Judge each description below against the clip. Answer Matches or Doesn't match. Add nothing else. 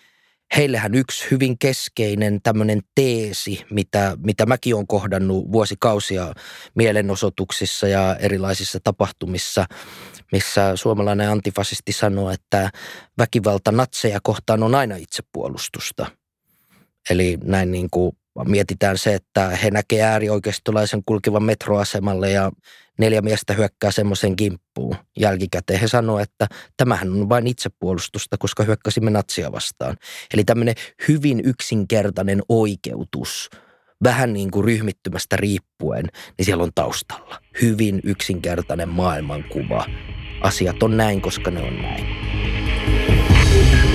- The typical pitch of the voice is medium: Doesn't match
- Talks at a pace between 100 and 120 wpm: Matches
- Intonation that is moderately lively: Doesn't match